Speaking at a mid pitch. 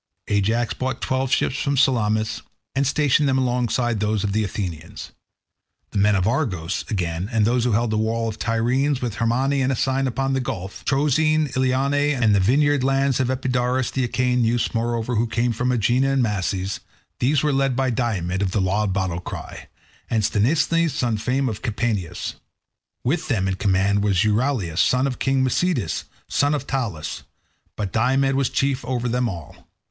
No: low, 120 Hz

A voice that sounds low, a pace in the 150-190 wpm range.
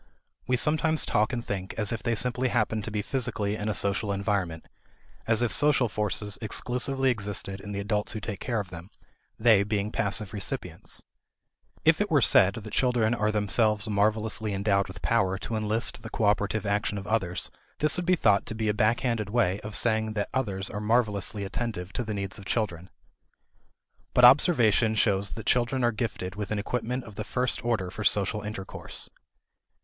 Yes: low, 105 Hz; average, 185 wpm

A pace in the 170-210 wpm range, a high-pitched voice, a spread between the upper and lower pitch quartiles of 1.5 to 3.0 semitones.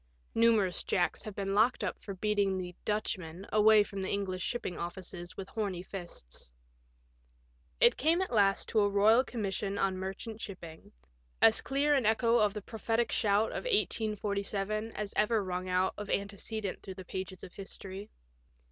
Yes: average, 175 wpm; high, 200 Hz; narrow, 2.6 semitones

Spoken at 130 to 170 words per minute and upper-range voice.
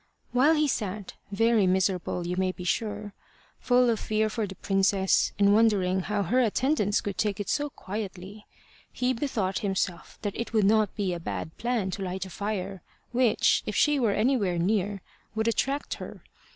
No: average, 180 wpm; high, 205 Hz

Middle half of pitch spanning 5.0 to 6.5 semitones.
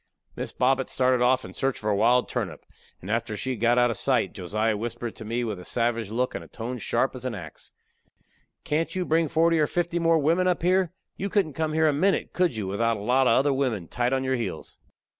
Yes: wide, 5.5 semitones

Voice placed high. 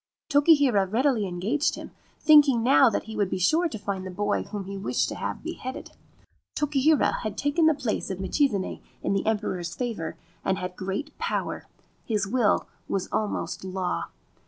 Yes: high, 215 Hz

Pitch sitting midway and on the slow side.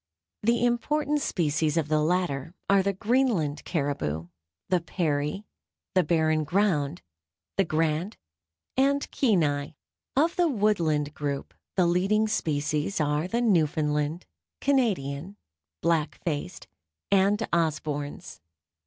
Yes: medium, 170 Hz; slow, 110 wpm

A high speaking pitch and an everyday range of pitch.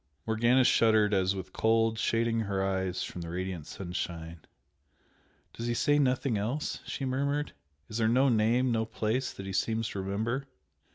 No: low, 110 Hz; average, 4.0 semitones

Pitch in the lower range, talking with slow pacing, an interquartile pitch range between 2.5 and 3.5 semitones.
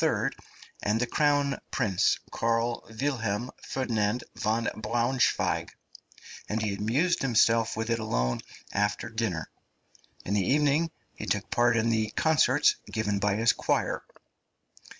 Yes: low, 115 Hz; slow, 125 wpm; average, 3.1 semitones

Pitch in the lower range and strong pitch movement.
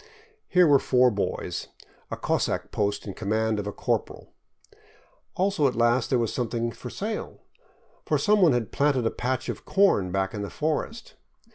Yes: low, 120 Hz; wide, 5.8 semitones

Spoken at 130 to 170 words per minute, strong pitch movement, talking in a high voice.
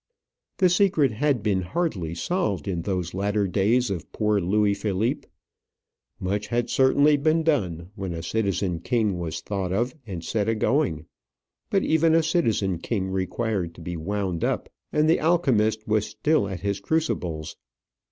No: average, 155 wpm; wide, 6.2 semitones; low, 105 Hz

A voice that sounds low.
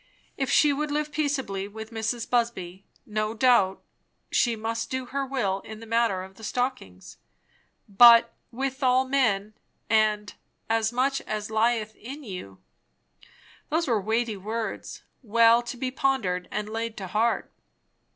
No: high, 230 Hz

